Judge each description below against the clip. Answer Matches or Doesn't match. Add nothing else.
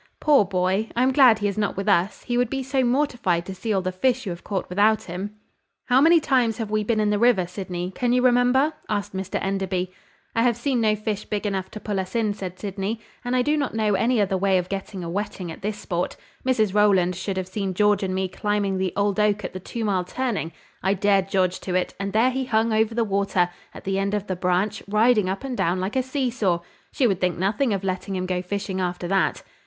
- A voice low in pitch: Doesn't match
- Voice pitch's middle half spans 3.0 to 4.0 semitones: Matches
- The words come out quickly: Matches